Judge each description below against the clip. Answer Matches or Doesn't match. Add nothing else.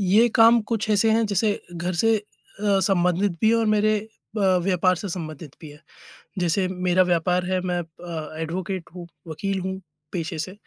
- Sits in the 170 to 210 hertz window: Matches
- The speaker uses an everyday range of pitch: Matches